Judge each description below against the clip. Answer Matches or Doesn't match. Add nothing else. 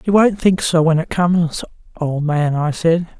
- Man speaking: Doesn't match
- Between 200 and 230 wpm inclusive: Matches